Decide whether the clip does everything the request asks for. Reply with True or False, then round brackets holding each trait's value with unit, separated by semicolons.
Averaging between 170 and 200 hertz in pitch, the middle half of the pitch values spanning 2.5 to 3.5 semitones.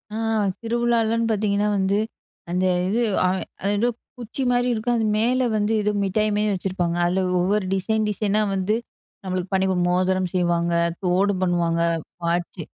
True (195 Hz; 3.0 semitones)